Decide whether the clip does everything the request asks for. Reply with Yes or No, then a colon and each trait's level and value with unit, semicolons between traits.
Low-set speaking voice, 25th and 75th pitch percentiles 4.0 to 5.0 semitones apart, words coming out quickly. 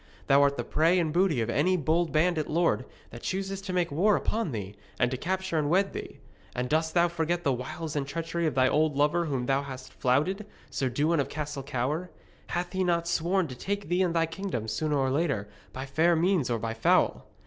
No: medium, 160 Hz; average, 4.3 semitones; fast, 220 wpm